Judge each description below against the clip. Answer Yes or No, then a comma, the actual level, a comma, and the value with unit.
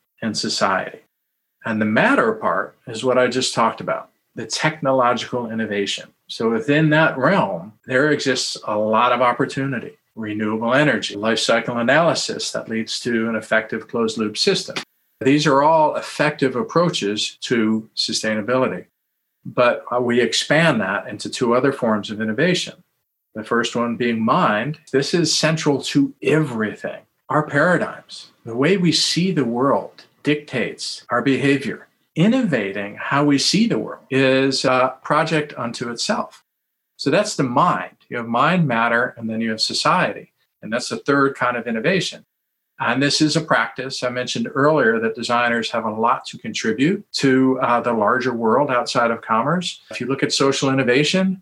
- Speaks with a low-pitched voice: Yes, low, 130 Hz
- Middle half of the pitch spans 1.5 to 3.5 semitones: No, average, 4.4 semitones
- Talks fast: No, average, 160 wpm